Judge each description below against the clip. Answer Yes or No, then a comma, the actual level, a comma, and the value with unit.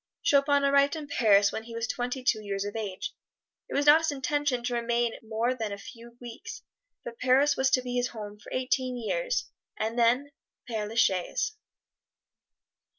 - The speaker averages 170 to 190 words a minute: Yes, average, 180 wpm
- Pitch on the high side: Yes, high, 245 Hz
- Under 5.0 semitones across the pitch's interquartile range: Yes, average, 3.8 semitones